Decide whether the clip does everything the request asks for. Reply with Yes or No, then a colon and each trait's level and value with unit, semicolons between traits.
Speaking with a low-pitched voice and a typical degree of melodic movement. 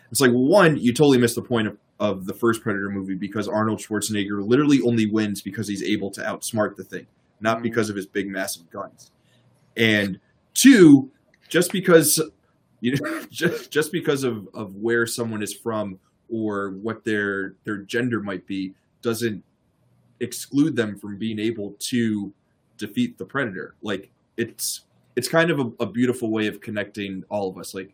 Yes: low, 110 Hz; average, 3.3 semitones